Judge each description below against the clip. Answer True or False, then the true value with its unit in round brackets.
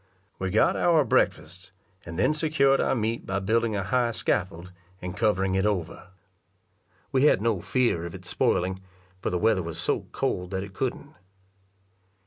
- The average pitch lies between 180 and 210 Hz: False (100 Hz)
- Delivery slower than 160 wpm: False (165 wpm)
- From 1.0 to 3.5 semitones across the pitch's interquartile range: False (4.4 semitones)